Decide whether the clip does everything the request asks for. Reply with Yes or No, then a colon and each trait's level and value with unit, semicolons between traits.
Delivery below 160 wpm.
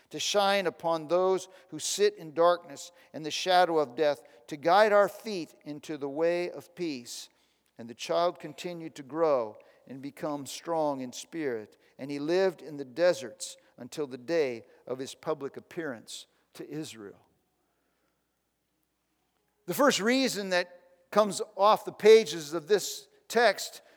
Yes: average, 150 wpm